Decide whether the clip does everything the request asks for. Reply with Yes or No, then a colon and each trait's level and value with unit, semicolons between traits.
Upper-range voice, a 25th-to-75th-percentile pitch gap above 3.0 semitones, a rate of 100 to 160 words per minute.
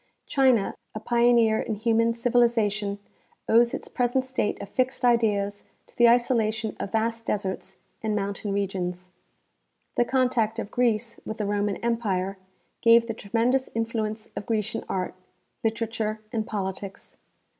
No: high, 225 Hz; narrow, 2.4 semitones; average, 140 wpm